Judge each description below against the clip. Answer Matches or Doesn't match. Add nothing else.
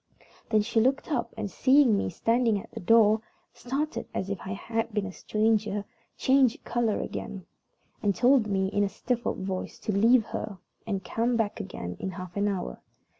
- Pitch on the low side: Doesn't match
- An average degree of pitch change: Matches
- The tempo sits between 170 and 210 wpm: Matches